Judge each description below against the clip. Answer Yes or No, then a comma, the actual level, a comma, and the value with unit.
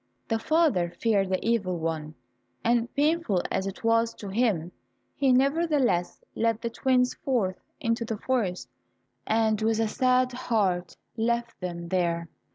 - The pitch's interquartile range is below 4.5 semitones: No, average, 5.3 semitones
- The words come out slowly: No, average, 145 wpm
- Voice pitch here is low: No, high, 225 Hz